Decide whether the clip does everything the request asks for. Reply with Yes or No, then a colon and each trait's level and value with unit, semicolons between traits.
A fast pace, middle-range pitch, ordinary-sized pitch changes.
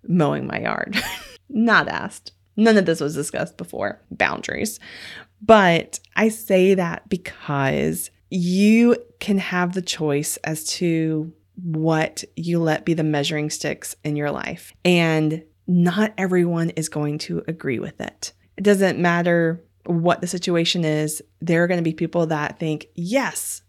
No: average, 150 wpm; medium, 170 Hz; average, 3.0 semitones